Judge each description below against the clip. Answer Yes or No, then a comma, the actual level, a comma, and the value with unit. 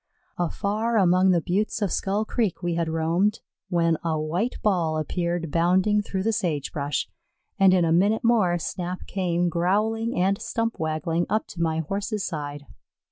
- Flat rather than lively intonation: No, average, 3.7 semitones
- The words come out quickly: No, average, 165 wpm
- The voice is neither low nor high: Yes, medium, 180 Hz